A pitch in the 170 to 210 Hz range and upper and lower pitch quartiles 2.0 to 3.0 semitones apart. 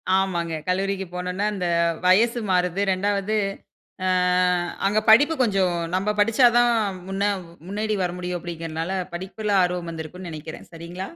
Yes: medium, 185 Hz; average, 2.7 semitones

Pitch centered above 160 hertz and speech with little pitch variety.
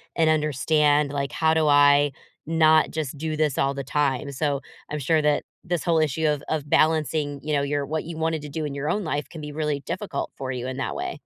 No: medium, 150 Hz; narrow, 1.8 semitones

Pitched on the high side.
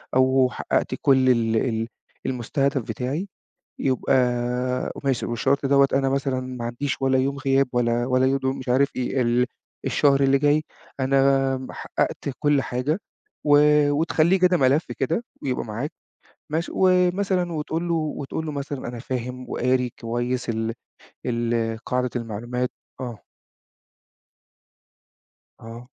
No: low, 130 Hz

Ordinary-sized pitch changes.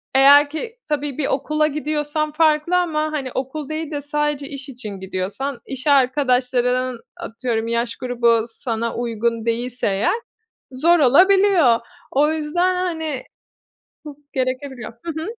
Yes: average, 3.8 semitones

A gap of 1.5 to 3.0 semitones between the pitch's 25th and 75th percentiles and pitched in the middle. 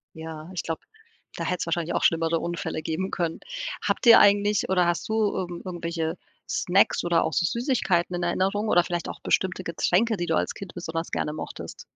Yes: narrow, 2.4 semitones; medium, 175 Hz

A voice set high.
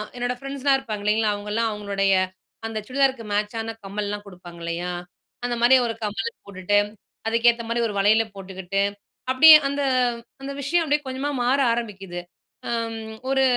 Yes: high, 225 Hz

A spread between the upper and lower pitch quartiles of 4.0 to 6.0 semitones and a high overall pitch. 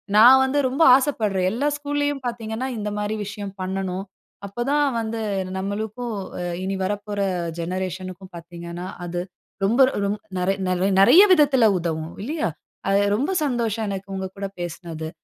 Yes: average, 4.5 semitones; high, 205 Hz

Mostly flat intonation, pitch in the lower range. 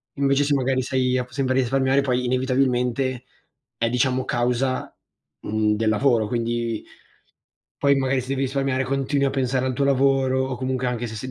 Yes: narrow, 1.6 semitones; low, 130 Hz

